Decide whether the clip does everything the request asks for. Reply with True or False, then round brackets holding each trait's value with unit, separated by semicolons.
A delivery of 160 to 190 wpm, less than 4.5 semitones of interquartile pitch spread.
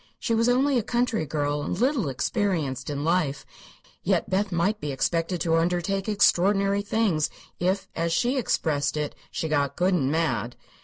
False (170 wpm; 5.5 semitones)